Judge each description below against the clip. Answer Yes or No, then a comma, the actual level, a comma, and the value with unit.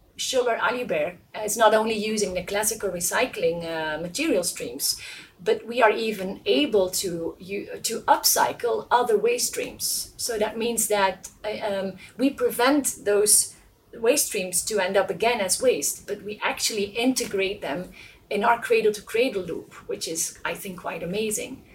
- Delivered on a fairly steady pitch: No, average, 3.8 semitones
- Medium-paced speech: Yes, average, 155 wpm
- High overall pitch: Yes, high, 210 Hz